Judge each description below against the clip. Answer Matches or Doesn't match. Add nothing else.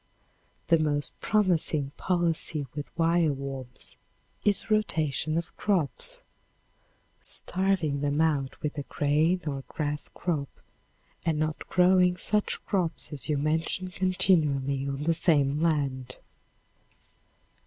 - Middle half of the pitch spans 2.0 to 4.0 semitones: Matches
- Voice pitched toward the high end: Doesn't match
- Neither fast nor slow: Doesn't match